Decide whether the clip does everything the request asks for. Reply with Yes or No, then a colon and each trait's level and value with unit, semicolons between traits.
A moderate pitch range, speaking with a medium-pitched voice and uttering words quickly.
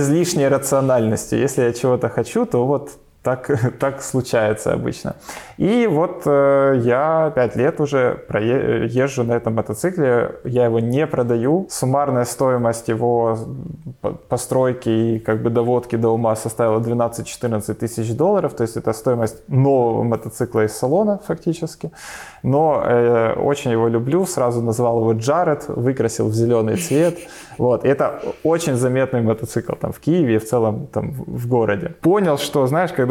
No: average, 3.7 semitones; low, 125 Hz; fast, 160 wpm